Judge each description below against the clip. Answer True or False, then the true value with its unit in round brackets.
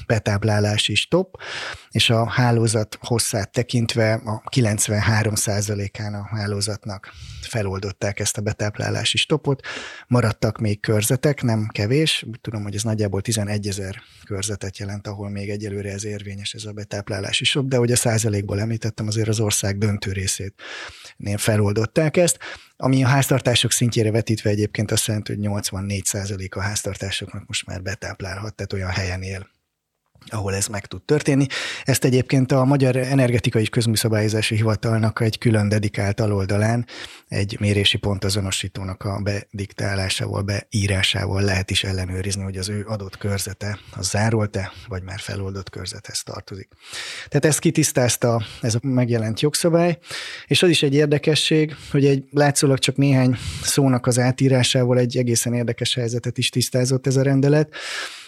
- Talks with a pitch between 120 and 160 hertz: False (110 Hz)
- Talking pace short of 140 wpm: False (145 wpm)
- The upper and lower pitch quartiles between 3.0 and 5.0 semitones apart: True (3.5 semitones)